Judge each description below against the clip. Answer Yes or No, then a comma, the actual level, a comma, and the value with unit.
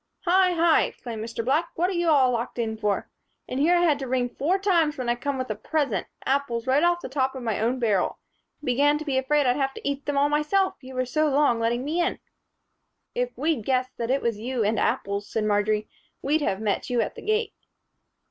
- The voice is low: No, very high, 265 Hz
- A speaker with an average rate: No, fast, 235 wpm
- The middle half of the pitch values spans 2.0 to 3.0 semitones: No, average, 4.6 semitones